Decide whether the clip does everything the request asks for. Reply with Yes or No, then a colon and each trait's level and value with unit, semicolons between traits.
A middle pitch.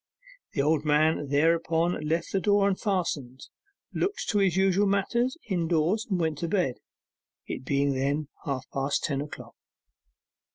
Yes: medium, 165 Hz